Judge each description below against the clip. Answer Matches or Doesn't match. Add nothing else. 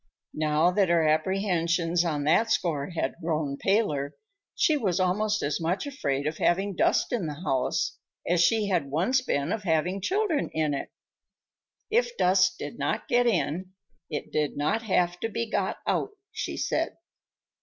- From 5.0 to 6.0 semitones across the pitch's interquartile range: Matches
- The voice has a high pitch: Doesn't match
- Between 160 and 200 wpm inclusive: Matches